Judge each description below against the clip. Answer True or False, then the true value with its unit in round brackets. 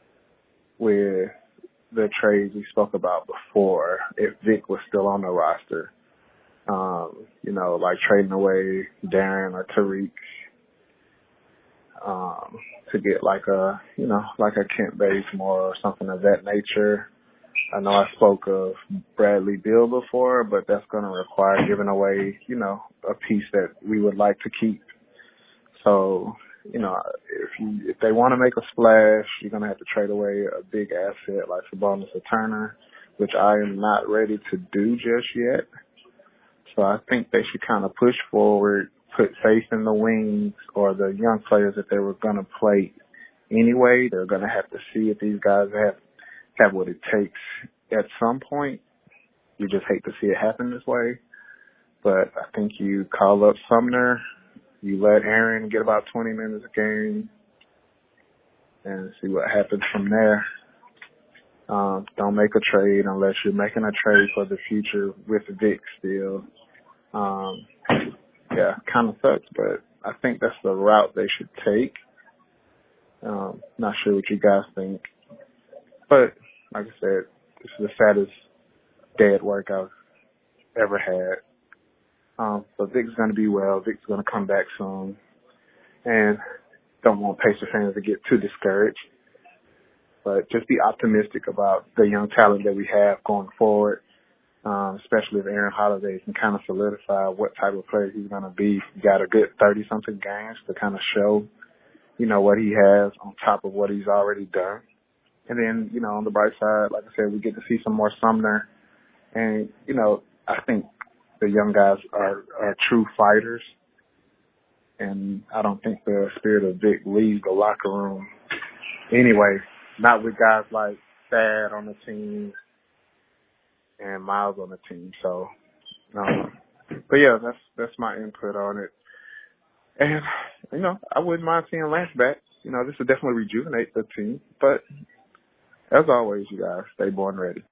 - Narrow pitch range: True (2.1 semitones)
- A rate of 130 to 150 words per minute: False (170 wpm)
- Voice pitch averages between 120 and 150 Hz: False (105 Hz)